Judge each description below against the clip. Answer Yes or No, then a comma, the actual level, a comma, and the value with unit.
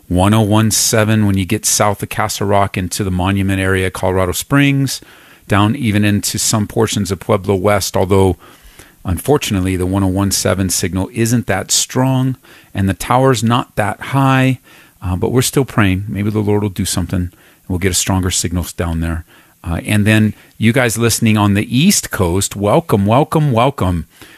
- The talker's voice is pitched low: Yes, low, 105 Hz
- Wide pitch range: No, average, 3.3 semitones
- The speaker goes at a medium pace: Yes, average, 165 wpm